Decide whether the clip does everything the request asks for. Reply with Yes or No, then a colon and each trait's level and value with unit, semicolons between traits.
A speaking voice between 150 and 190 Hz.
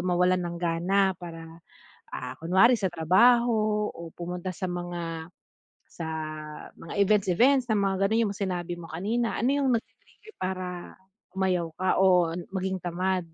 Yes: medium, 185 Hz